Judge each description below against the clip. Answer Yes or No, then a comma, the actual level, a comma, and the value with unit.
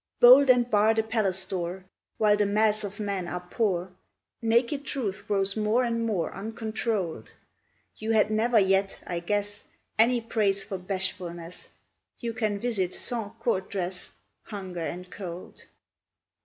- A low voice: No, high, 205 Hz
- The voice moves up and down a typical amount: Yes, average, 3.0 semitones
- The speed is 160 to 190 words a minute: No, average, 140 wpm